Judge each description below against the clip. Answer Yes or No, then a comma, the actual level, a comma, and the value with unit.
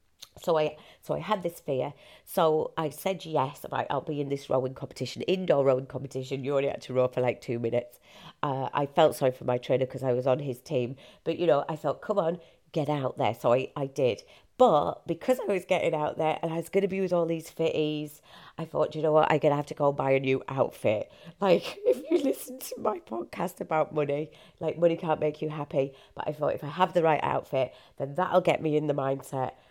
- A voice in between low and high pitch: Yes, medium, 150 Hz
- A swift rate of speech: Yes, fast, 240 wpm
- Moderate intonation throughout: Yes, average, 3.6 semitones